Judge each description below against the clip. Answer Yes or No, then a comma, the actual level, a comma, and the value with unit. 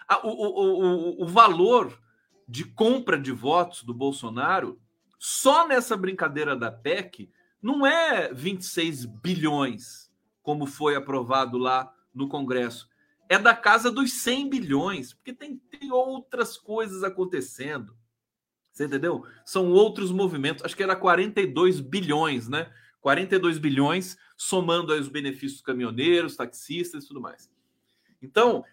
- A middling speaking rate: Yes, average, 130 wpm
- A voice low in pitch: No, medium, 175 Hz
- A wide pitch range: Yes, wide, 7.2 semitones